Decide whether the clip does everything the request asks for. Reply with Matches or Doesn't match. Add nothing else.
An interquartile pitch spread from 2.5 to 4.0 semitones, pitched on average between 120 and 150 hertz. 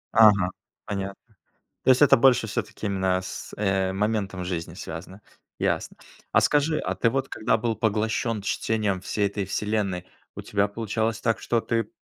Doesn't match